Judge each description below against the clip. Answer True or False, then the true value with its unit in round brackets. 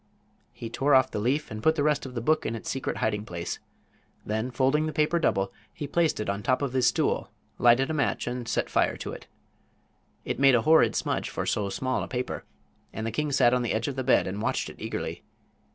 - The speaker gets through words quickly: True (240 wpm)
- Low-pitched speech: True (125 Hz)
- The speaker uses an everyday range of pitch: True (4.3 semitones)